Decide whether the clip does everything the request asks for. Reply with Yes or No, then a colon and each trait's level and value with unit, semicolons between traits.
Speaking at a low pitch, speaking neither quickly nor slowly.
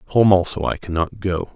Yes: very low, 95 Hz; average, 190 wpm